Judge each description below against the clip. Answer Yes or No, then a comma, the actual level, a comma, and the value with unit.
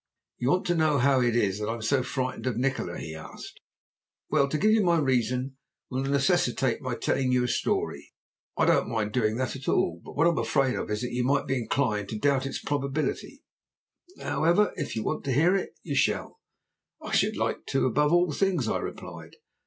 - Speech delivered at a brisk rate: Yes, fast, 215 wpm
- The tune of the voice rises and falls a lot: No, average, 3.4 semitones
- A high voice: No, low, 130 Hz